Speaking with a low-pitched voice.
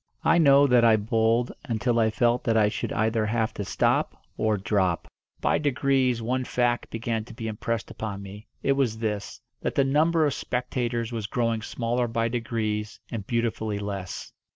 Yes: low, 115 Hz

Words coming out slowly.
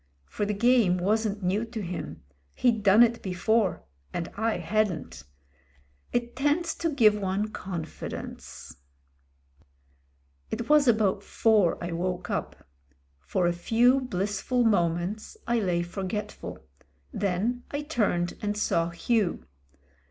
Yes: slow, 130 wpm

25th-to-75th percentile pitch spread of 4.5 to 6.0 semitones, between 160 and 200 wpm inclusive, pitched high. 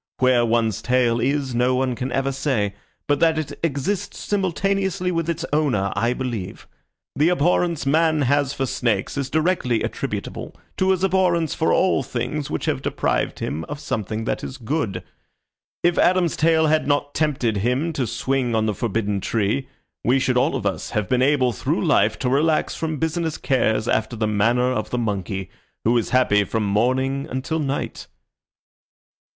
No: average, 5.2 semitones; average, 170 wpm; low, 130 Hz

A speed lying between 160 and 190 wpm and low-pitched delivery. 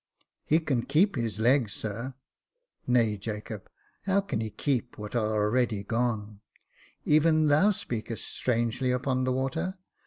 No: average, 150 wpm; low, 125 Hz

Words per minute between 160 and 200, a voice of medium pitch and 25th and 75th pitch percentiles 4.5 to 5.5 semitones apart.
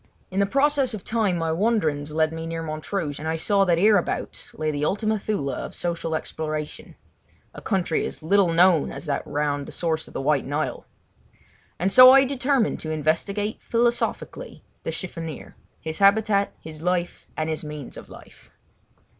Yes: average, 165 wpm; medium, 170 Hz; average, 4.8 semitones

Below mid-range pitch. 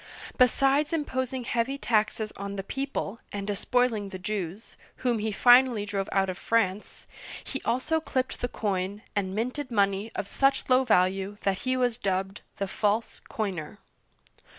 No: high, 215 Hz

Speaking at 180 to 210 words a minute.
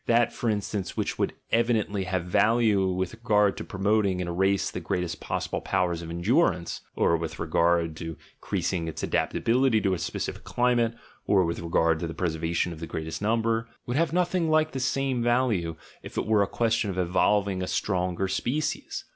Yes: average, 185 wpm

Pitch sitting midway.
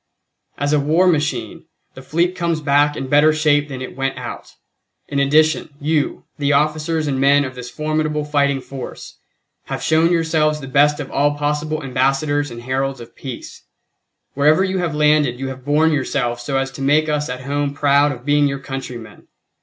Yes: medium, 145 Hz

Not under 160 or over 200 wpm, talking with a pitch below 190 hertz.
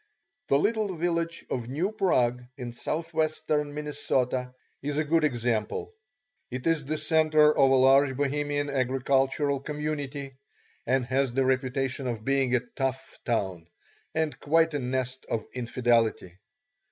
No: slow, 135 wpm; low, 135 Hz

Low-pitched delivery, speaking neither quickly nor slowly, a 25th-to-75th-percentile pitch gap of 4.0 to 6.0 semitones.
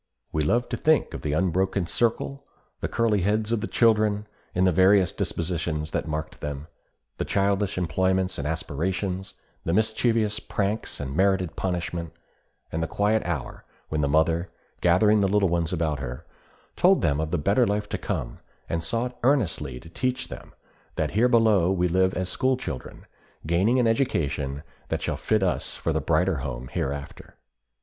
Yes: very low, 95 Hz; average, 170 wpm; average, 5.0 semitones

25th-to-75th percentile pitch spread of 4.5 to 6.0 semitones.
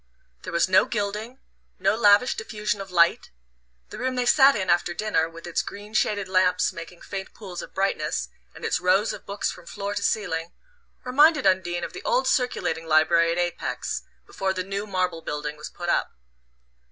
No: average, 3.6 semitones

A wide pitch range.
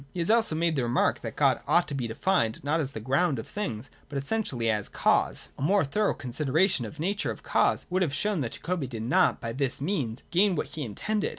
Yes: wide, 7.0 semitones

